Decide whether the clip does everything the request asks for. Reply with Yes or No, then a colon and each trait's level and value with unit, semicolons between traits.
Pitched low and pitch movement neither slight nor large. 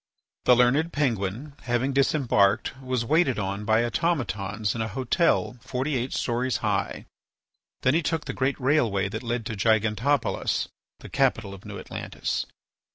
Yes: low, 125 Hz; average, 3.8 semitones